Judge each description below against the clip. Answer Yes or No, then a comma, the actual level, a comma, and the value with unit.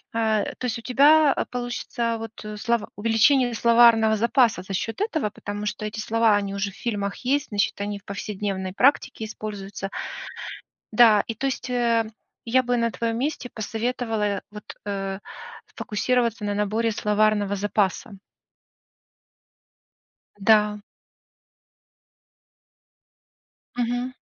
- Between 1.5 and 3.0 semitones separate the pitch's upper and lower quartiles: Yes, narrow, 2.6 semitones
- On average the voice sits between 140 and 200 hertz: No, high, 220 Hz